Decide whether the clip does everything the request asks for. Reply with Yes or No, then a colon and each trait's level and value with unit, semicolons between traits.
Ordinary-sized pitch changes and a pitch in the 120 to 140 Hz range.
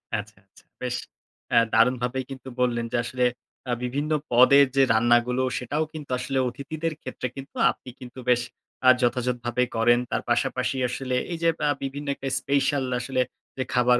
No: narrow, 2.0 semitones; low, 125 Hz